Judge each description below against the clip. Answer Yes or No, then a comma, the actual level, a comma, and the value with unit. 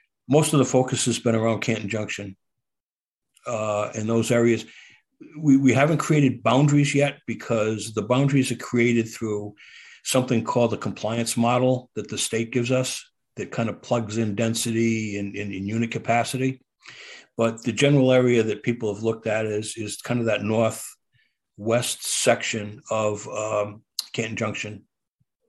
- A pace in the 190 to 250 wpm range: No, average, 160 wpm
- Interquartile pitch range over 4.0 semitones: No, average, 2.8 semitones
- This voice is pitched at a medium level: No, low, 115 Hz